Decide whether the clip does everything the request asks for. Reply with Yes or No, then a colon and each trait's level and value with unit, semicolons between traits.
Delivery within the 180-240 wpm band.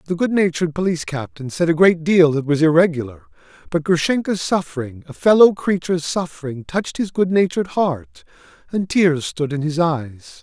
No: average, 160 wpm